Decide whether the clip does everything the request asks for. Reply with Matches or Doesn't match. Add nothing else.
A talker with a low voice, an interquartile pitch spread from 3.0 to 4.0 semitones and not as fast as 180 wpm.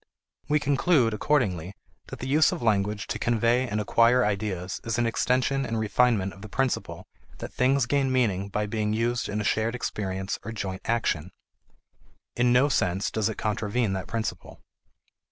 Matches